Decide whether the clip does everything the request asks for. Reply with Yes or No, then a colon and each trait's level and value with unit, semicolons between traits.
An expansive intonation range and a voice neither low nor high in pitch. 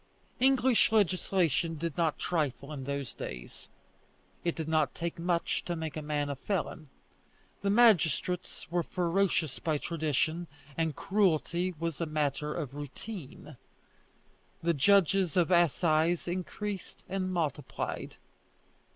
No: average, 3.3 semitones; medium, 165 Hz